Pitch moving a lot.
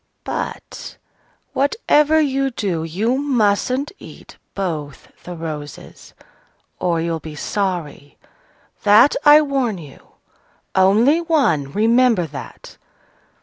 Yes: wide, 8.7 semitones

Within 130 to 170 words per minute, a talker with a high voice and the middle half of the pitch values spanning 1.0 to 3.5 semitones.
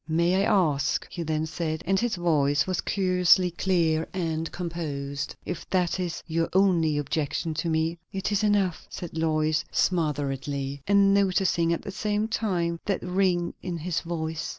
No: average, 160 wpm; medium, 170 Hz; average, 2.9 semitones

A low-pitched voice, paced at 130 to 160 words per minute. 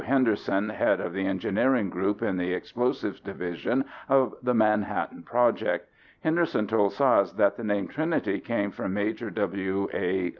Yes: low, 105 Hz; average, 150 wpm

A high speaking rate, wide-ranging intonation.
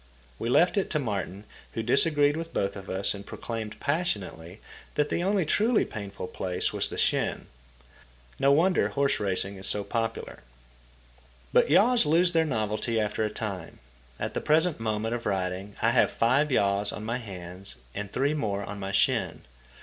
No: average, 175 wpm; wide, 6.8 semitones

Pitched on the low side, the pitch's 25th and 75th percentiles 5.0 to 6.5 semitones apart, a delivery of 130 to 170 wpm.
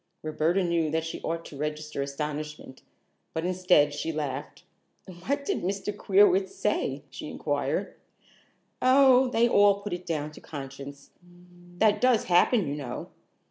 No: medium, 170 Hz; wide, 5.5 semitones; average, 140 wpm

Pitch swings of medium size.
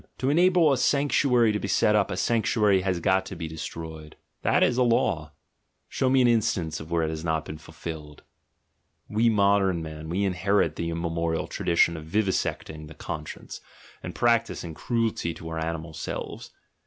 No: wide, 5.7 semitones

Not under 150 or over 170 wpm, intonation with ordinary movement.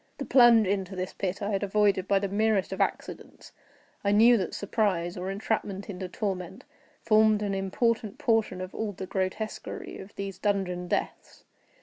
No: average, 165 wpm; narrow, 2.3 semitones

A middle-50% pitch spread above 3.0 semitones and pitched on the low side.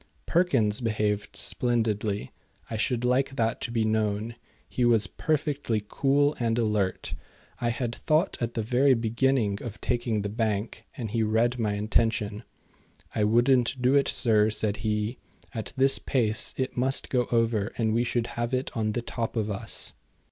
No: narrow, 2.6 semitones; low, 115 Hz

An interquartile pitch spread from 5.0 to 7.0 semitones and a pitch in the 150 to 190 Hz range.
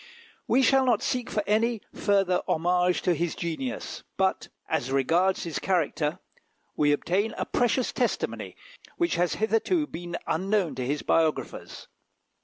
Yes: wide, 5.4 semitones; medium, 185 Hz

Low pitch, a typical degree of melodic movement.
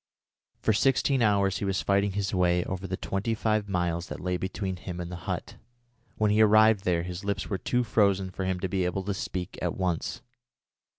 No: very low, 95 Hz; narrow, 2.3 semitones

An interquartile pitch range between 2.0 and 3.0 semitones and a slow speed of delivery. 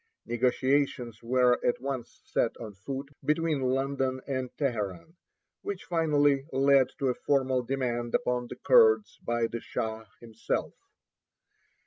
Yes: average, 2.7 semitones; slow, 125 wpm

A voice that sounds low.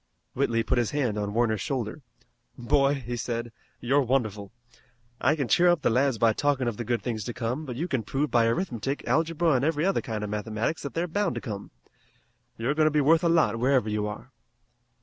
Yes: low, 125 Hz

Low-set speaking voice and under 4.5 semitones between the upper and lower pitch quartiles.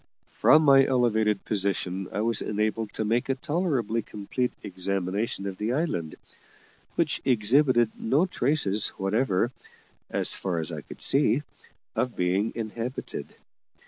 No: low, 110 Hz; average, 4.8 semitones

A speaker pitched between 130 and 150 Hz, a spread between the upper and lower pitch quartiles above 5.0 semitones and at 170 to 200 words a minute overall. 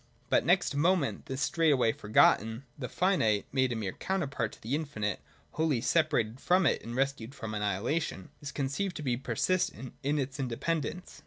Yes: low, 135 Hz; wide, 5.6 semitones; average, 175 wpm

